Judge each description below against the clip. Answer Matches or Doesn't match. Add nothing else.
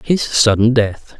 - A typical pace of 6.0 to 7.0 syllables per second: Doesn't match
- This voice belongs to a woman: Doesn't match